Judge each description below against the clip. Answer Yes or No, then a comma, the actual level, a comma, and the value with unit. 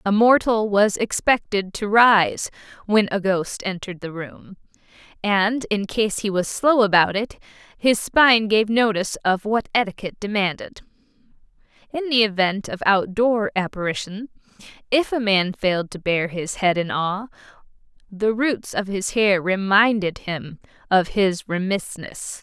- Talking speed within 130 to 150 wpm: Yes, average, 145 wpm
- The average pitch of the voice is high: Yes, high, 205 Hz